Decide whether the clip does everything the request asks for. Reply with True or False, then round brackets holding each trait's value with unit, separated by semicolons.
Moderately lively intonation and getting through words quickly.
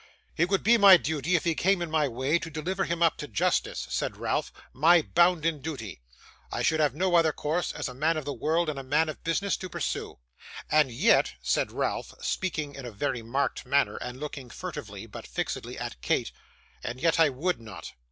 True (4.1 semitones; 210 wpm)